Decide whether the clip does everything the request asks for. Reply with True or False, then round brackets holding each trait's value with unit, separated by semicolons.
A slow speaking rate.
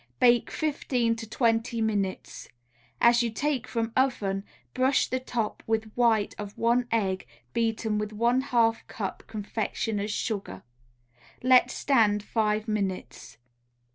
True (125 wpm)